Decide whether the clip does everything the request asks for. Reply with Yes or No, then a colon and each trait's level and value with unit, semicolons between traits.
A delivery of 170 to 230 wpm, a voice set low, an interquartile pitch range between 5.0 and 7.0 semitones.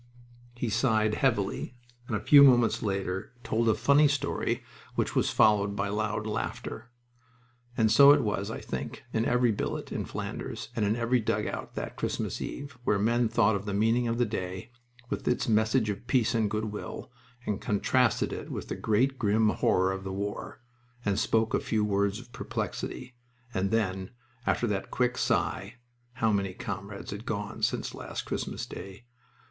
No: average, 175 wpm; low, 110 Hz; average, 3.1 semitones